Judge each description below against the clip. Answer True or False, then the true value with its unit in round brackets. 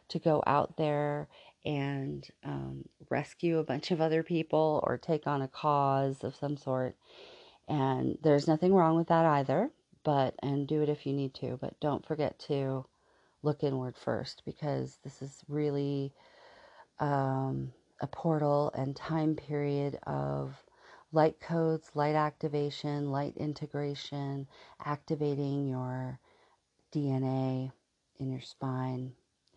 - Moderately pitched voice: True (145 Hz)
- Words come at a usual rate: False (130 wpm)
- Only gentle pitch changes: True (2.3 semitones)